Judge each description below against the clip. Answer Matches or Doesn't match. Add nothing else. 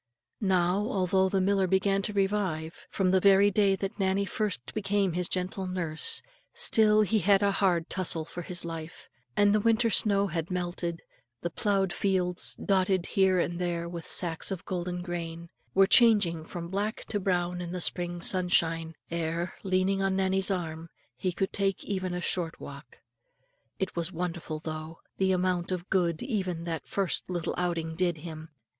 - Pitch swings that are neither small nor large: Doesn't match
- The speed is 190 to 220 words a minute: Doesn't match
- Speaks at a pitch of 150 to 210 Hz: Matches